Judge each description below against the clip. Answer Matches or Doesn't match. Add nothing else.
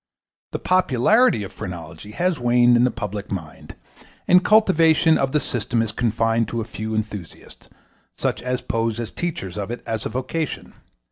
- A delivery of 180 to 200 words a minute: Doesn't match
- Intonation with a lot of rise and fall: Matches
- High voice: Doesn't match